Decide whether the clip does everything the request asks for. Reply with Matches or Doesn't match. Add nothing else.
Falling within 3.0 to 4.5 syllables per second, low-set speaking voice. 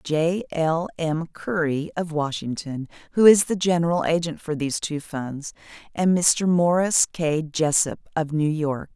Doesn't match